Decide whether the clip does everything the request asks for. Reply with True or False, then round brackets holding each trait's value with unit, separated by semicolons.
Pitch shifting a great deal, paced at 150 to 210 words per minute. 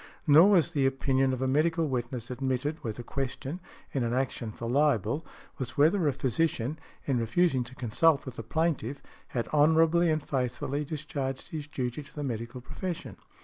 False (3.7 semitones; 175 wpm)